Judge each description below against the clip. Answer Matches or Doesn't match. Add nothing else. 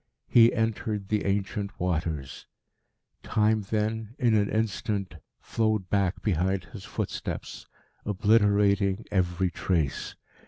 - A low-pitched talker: Matches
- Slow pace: Matches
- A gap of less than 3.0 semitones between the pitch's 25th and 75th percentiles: Matches